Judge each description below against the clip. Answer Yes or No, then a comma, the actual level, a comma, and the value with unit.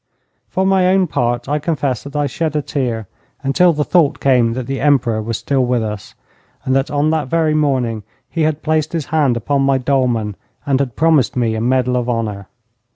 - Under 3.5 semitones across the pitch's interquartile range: No, average, 4.0 semitones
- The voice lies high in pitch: No, low, 135 Hz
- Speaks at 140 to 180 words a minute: No, fast, 205 wpm